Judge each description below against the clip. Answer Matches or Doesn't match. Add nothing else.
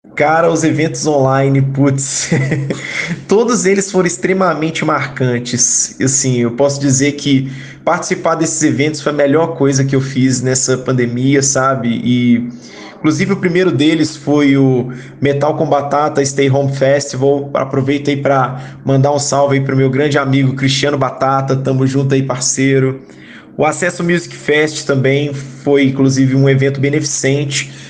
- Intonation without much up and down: Matches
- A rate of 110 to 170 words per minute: Matches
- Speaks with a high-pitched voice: Doesn't match